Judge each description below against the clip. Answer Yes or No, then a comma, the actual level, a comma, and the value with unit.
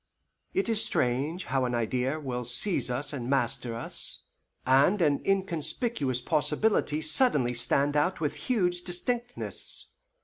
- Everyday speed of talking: No, slow, 130 wpm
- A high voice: No, medium, 150 Hz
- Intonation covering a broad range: Yes, wide, 6.8 semitones